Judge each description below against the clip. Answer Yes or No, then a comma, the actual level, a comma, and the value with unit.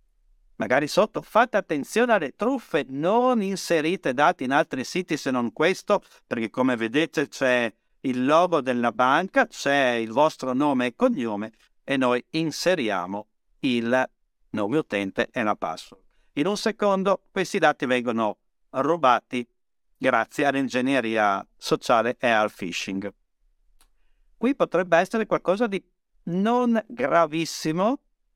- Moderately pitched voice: Yes, medium, 160 Hz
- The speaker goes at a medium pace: Yes, average, 125 wpm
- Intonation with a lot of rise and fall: Yes, wide, 8.4 semitones